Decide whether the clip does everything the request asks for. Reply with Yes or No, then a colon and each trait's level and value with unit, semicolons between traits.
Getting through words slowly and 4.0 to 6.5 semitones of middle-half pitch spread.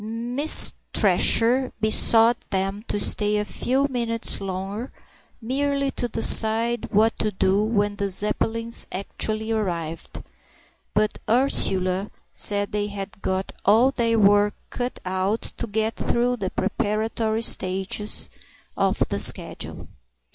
No: slow, 120 wpm; narrow, 2.6 semitones